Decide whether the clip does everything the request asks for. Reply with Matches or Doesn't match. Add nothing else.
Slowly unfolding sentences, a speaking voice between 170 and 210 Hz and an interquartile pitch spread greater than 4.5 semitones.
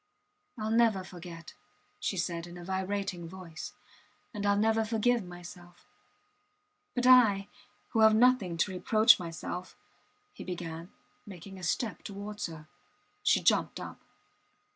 Doesn't match